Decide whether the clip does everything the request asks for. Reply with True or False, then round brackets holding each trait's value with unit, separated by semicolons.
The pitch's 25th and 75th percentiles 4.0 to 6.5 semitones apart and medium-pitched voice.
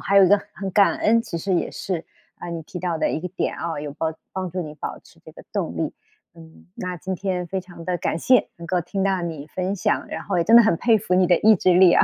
False (2.5 semitones; 180 Hz)